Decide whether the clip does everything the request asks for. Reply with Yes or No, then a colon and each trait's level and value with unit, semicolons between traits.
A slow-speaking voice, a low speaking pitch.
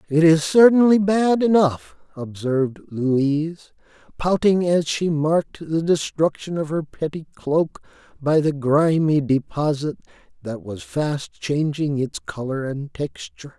No: slow, 130 wpm; medium, 155 Hz